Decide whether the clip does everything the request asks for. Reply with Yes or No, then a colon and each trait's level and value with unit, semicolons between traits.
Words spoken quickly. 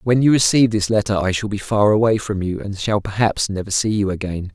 Yes: fast, 250 wpm